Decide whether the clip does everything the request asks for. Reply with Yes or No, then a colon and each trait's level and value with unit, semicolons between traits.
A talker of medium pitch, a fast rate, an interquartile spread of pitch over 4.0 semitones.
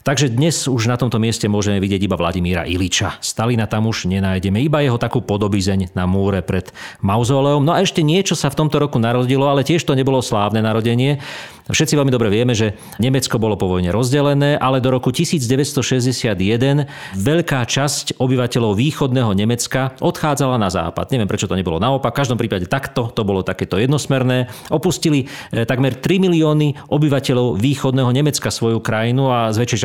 No: low, 125 Hz; fast, 170 wpm; average, 4.6 semitones